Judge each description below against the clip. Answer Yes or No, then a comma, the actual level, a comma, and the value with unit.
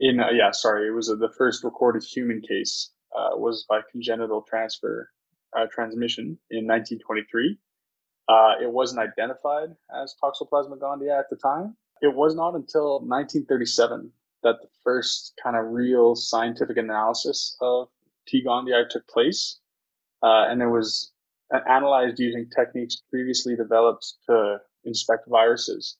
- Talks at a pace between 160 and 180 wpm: No, average, 140 wpm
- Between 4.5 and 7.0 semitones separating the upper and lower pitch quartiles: No, average, 3.1 semitones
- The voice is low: Yes, low, 120 Hz